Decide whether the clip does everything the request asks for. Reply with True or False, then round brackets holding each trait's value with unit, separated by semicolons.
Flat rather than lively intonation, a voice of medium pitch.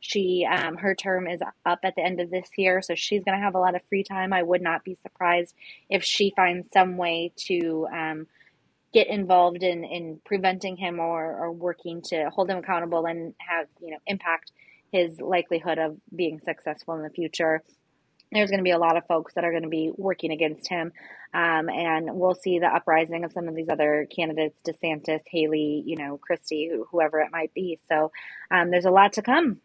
True (2.3 semitones; 170 Hz)